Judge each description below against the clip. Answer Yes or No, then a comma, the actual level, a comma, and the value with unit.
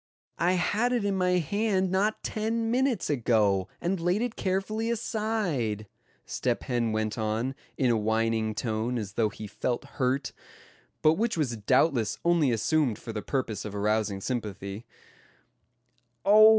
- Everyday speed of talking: Yes, average, 150 wpm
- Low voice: Yes, low, 130 Hz